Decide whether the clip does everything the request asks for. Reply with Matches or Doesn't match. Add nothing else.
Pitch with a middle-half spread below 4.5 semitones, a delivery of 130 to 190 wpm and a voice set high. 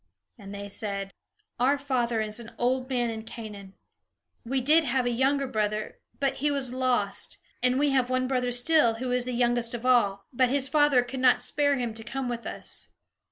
Doesn't match